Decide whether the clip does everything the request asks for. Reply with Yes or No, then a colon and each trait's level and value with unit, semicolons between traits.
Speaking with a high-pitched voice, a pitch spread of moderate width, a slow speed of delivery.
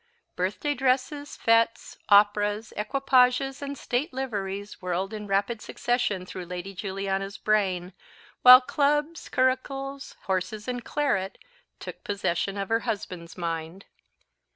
Yes: high, 210 Hz; average, 5.0 semitones; slow, 115 wpm